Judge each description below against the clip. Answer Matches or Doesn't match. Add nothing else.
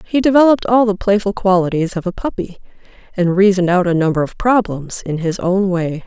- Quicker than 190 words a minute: Matches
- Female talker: Matches